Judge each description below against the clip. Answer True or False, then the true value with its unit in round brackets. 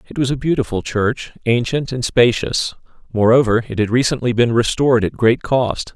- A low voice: True (120 Hz)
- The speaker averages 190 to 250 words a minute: False (170 wpm)